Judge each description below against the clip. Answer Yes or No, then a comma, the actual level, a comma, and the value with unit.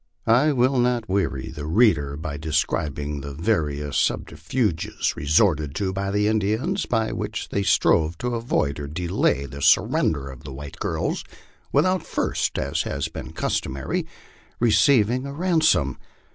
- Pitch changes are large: Yes, wide, 8.6 semitones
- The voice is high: No, very low, 95 Hz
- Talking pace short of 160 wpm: Yes, average, 150 wpm